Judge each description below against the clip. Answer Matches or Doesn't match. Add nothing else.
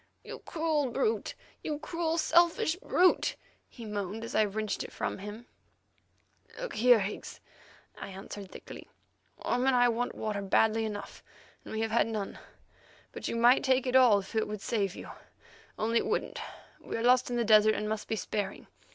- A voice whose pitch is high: Matches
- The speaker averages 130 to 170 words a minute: Doesn't match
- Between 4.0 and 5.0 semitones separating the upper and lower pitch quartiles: Doesn't match